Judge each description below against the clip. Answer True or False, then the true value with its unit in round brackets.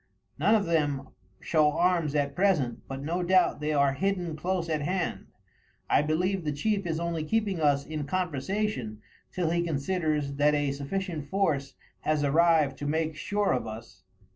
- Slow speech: False (165 wpm)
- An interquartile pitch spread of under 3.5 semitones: False (4.0 semitones)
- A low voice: False (155 Hz)